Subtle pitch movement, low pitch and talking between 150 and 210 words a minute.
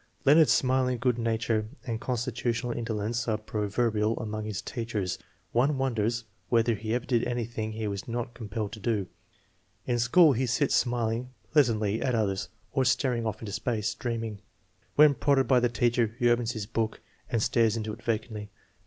Yes: narrow, 2.1 semitones; low, 115 Hz; average, 170 wpm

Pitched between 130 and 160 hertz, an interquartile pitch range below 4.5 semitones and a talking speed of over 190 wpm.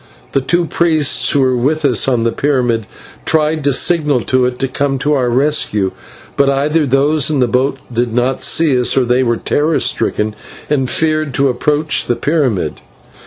No: low, 135 Hz; average, 3.4 semitones; average, 185 wpm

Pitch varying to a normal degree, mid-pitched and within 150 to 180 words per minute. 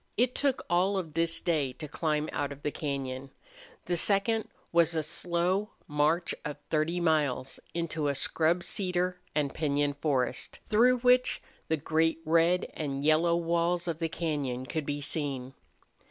Yes: average, 3.1 semitones; medium, 160 Hz; average, 155 wpm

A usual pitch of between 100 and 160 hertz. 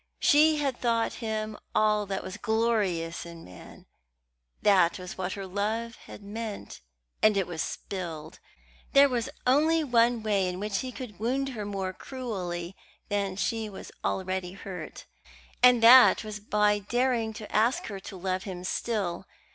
No: high, 210 Hz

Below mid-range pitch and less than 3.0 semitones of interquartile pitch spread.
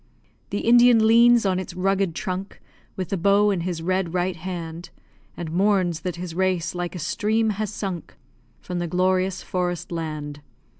No: medium, 185 Hz; narrow, 2.4 semitones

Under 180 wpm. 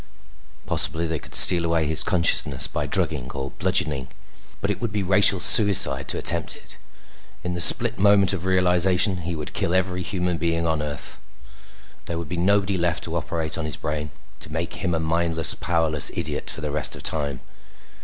No: average, 185 wpm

